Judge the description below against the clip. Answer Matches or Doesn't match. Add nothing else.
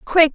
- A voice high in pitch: Matches